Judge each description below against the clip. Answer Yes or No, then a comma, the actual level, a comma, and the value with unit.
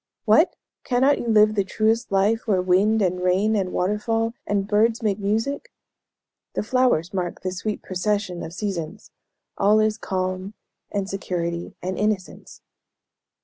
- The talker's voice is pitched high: Yes, high, 205 Hz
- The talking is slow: No, average, 145 wpm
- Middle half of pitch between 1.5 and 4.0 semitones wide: Yes, average, 2.8 semitones